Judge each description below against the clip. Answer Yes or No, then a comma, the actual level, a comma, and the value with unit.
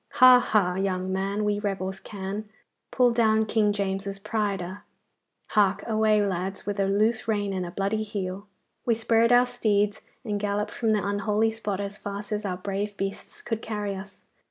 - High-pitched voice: Yes, high, 205 Hz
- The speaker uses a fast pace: No, average, 180 wpm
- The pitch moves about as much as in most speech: No, narrow, 1.8 semitones